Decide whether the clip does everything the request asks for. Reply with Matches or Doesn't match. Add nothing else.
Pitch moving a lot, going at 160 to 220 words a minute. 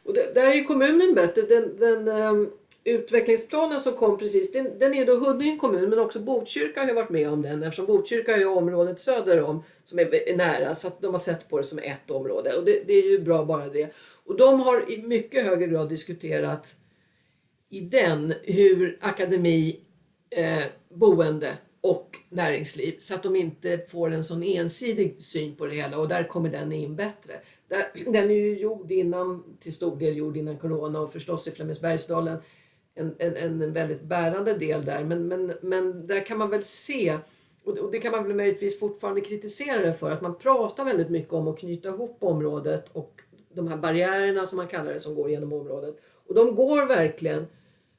Matches